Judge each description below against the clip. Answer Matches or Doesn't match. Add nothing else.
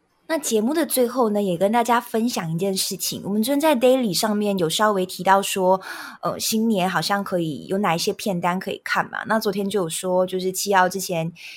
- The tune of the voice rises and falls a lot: Doesn't match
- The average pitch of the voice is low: Doesn't match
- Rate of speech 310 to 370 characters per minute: Matches